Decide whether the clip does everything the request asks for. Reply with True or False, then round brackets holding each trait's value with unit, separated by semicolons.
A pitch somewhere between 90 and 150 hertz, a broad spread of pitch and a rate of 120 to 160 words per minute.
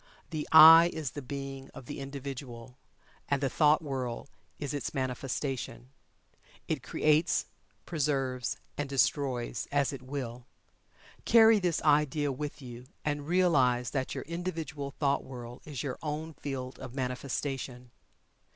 False (140 Hz; 2.9 semitones; 135 wpm)